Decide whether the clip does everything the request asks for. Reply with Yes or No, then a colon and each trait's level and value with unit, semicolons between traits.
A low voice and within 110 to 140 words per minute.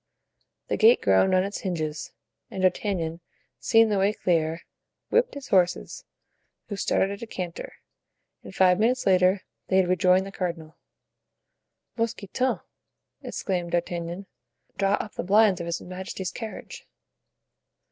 No: medium, 185 Hz; slow, 135 wpm